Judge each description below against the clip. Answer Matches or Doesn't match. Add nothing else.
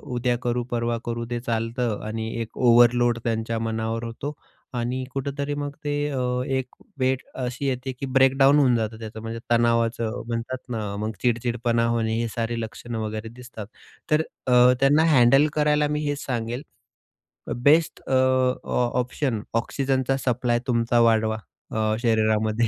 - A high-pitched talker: Doesn't match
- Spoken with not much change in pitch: Matches